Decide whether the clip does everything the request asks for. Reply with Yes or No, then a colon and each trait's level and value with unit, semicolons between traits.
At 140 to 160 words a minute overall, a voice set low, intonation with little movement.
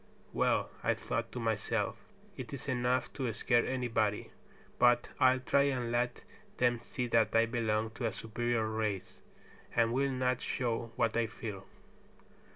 Yes: average, 155 wpm; low, 120 Hz; narrow, 2.0 semitones